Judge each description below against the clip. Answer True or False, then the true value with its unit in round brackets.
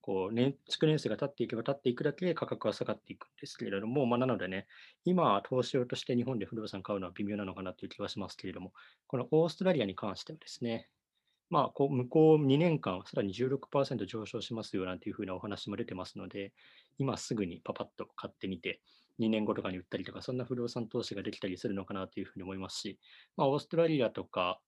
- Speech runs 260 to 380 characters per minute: False (470 characters per minute)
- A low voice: True (115 Hz)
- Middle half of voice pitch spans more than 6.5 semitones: False (5.5 semitones)